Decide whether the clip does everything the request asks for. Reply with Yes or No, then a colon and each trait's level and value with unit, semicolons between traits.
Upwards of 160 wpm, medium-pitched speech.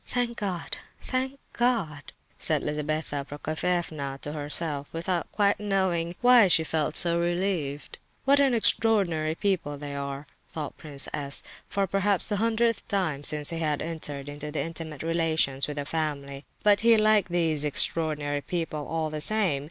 No: average, 145 wpm; medium, 165 Hz